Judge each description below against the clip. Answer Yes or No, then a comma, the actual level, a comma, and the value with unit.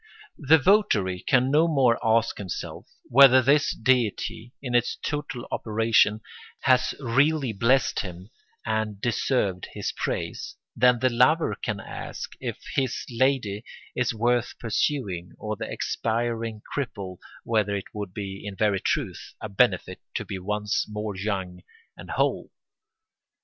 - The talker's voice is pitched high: No, low, 115 Hz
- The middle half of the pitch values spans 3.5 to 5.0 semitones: Yes, average, 4.0 semitones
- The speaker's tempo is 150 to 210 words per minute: No, slow, 135 wpm